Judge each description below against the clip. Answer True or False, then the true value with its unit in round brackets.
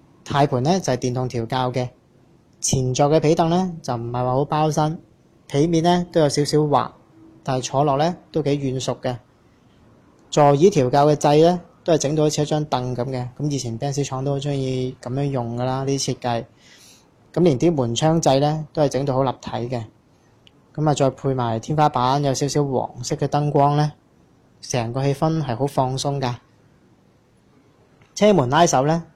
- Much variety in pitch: False (3.1 semitones)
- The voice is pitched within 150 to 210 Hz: False (140 Hz)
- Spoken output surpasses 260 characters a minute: False (255 characters per minute)